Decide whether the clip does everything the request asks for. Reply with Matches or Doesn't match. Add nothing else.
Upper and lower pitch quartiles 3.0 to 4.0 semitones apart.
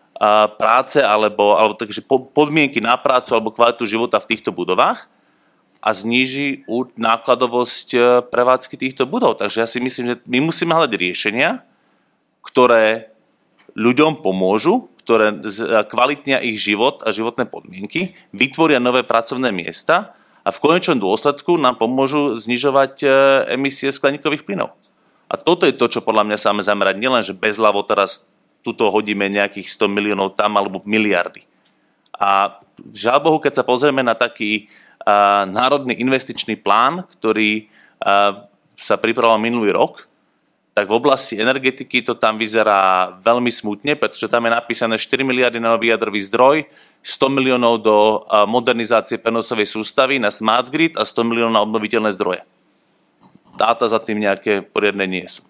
Matches